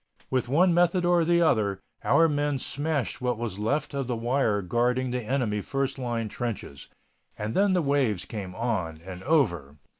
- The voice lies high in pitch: No, low, 125 Hz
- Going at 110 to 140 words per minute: No, average, 175 wpm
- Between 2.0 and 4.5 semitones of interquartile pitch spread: No, wide, 5.4 semitones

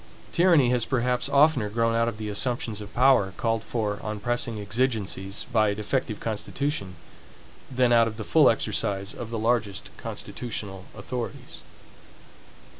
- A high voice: No, low, 115 Hz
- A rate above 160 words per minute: No, average, 145 wpm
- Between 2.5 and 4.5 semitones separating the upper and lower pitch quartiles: Yes, average, 3.1 semitones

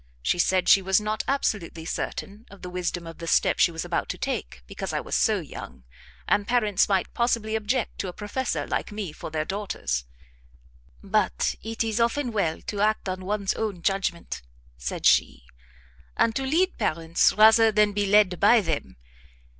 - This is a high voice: Yes, high, 200 Hz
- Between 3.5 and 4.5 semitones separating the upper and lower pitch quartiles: Yes, average, 4.1 semitones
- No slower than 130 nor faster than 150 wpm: No, average, 180 wpm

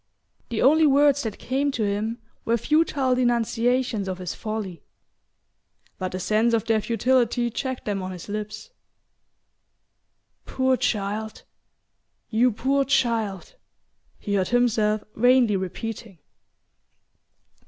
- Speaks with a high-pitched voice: Yes, high, 230 Hz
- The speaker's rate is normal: No, slow, 115 wpm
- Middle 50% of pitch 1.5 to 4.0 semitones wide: Yes, average, 3.5 semitones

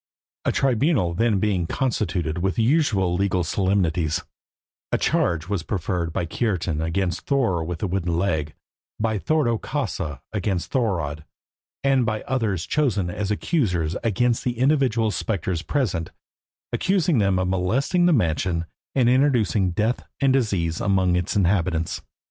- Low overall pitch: Yes, low, 100 Hz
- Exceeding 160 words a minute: No, average, 140 wpm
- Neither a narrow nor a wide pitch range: No, wide, 5.8 semitones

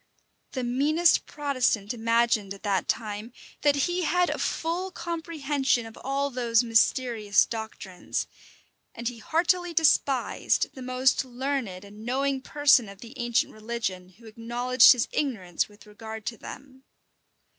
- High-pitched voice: Yes, high, 245 Hz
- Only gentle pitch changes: No, average, 4.1 semitones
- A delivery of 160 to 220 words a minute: No, average, 140 wpm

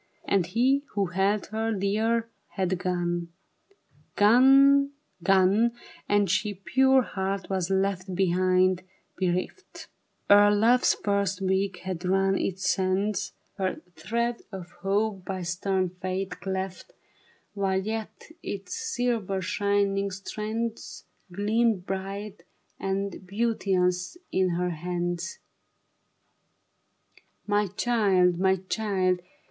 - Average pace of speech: No, slow, 105 wpm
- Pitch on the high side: Yes, high, 195 Hz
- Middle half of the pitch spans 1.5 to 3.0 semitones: Yes, narrow, 2.4 semitones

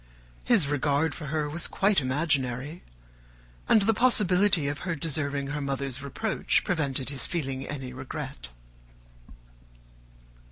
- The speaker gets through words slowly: Yes, slow, 120 wpm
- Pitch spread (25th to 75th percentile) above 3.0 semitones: Yes, average, 3.8 semitones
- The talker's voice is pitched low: No, medium, 145 Hz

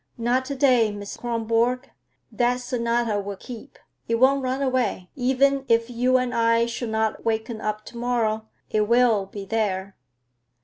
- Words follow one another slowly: No, average, 160 wpm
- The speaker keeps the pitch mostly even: Yes, narrow, 2.3 semitones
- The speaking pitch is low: No, high, 235 Hz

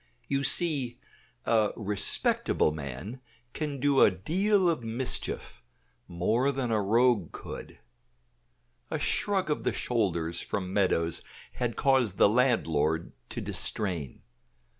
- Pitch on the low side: Yes, low, 115 Hz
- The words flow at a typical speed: No, slow, 120 wpm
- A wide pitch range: Yes, wide, 6.7 semitones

